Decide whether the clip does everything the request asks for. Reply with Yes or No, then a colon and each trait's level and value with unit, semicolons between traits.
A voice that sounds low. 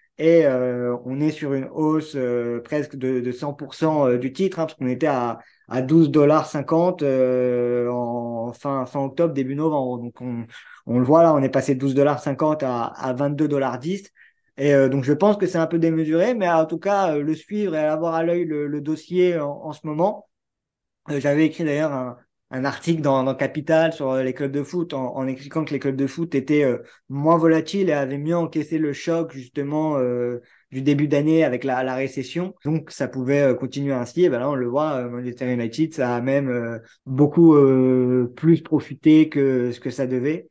No: medium, 145 Hz